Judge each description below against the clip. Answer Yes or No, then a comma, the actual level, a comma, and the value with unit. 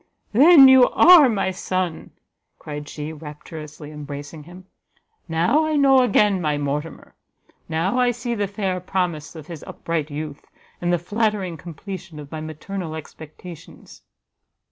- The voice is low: No, medium, 175 Hz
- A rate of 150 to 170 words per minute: No, average, 140 wpm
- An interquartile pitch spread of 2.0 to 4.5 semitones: No, average, 5.2 semitones